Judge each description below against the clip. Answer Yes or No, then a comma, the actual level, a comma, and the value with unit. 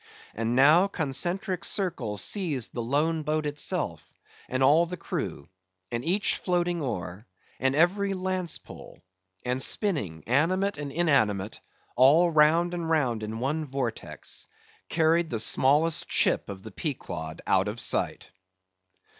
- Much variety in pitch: Yes, wide, 6.4 semitones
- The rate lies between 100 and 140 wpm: Yes, slow, 135 wpm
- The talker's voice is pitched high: No, medium, 150 Hz